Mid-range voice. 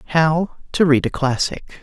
Yes: medium, 150 Hz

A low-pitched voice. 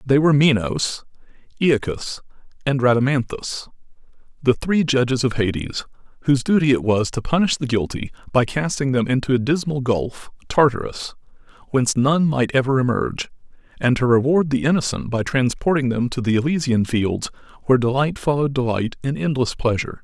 Yes: low, 130 Hz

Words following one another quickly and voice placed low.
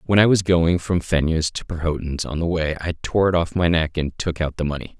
Yes: fast, 265 wpm; very low, 85 Hz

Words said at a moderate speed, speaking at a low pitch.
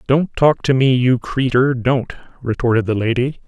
Yes: average, 175 wpm; low, 125 Hz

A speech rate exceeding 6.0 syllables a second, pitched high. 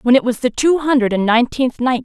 Yes: 6.2 syllables/s; very high, 250 Hz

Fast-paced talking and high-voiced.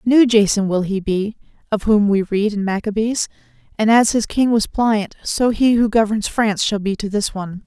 Yes: fast, 210 wpm; high, 215 Hz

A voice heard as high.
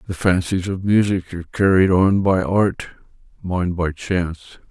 No: very low, 90 Hz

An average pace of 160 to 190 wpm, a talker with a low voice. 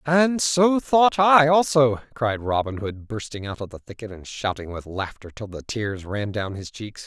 No: fast, 205 wpm; low, 120 Hz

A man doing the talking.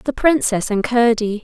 No: female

